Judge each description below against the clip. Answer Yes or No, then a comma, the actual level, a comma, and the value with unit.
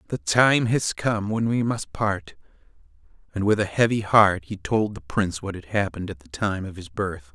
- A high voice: No, low, 100 Hz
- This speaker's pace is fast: Yes, fast, 210 wpm